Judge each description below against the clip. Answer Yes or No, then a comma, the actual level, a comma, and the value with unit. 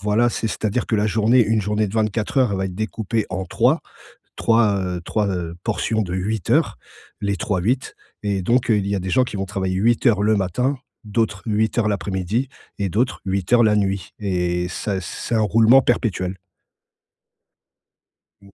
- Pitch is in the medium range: No, low, 105 Hz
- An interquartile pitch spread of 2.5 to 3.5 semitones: Yes, average, 2.9 semitones